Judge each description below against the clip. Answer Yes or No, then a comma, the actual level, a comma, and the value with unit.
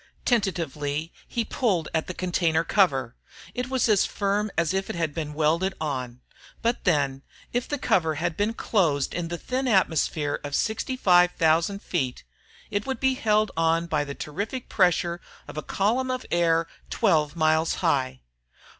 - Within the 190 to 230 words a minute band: No, average, 160 wpm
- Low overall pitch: No, medium, 170 Hz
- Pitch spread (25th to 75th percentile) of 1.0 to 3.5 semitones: No, average, 5.0 semitones